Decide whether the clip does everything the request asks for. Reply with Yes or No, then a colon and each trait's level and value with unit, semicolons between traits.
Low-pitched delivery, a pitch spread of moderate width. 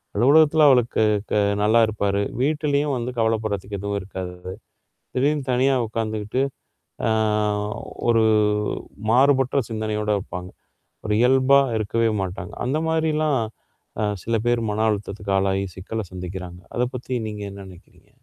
Yes: low, 110 Hz; average, 4.5 semitones